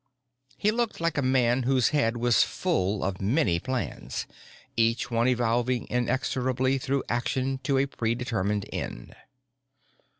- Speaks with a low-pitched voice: Yes, low, 125 Hz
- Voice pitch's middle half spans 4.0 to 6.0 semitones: No, narrow, 2.5 semitones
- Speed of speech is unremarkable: No, slow, 130 wpm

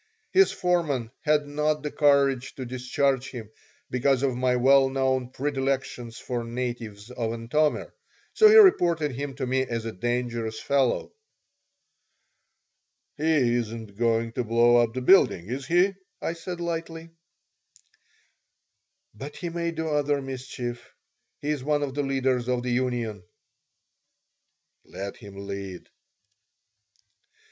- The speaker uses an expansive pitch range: No, average, 3.6 semitones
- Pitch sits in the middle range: No, low, 130 Hz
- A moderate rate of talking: No, slow, 130 wpm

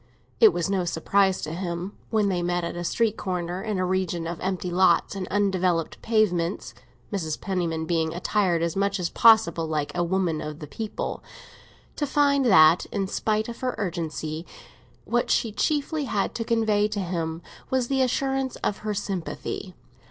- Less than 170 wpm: No, average, 175 wpm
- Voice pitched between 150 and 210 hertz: Yes, high, 190 Hz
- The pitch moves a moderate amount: Yes, average, 4.1 semitones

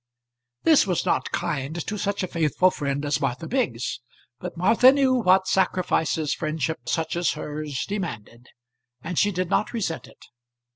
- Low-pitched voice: No, medium, 170 Hz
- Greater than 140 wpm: Yes, average, 155 wpm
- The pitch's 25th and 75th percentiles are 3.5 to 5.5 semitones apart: Yes, average, 4.8 semitones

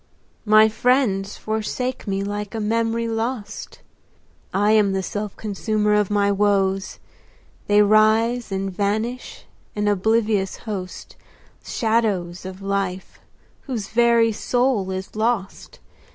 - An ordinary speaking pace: No, slow, 115 wpm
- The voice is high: Yes, high, 210 Hz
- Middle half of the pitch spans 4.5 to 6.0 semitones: No, narrow, 2.5 semitones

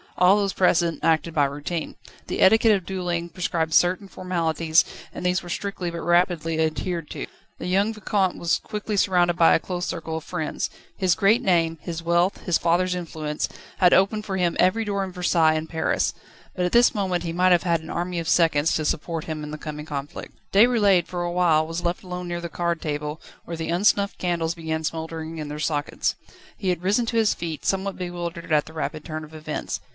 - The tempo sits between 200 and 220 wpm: Yes, fast, 205 wpm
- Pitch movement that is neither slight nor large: No, narrow, 2.3 semitones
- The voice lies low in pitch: No, medium, 175 Hz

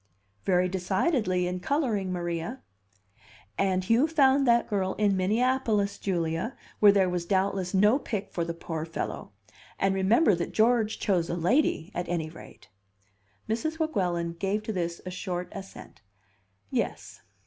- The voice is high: Yes, high, 195 Hz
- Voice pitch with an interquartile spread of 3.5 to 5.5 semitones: Yes, average, 4.0 semitones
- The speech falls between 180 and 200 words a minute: No, average, 145 wpm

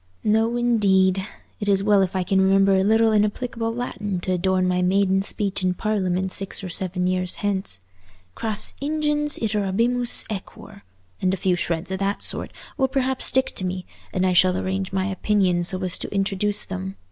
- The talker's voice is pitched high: Yes, high, 195 Hz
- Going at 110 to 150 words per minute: No, average, 180 wpm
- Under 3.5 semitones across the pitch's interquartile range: Yes, narrow, 2.5 semitones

